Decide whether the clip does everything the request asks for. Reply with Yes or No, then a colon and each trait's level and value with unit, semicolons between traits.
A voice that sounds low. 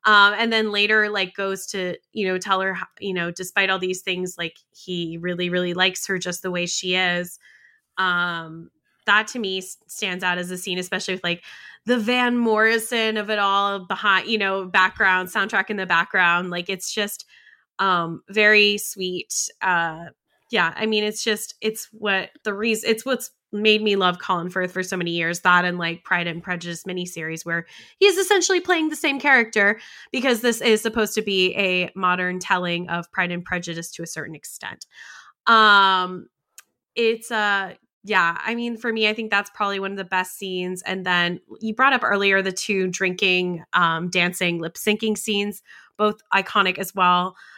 No: high, 190 Hz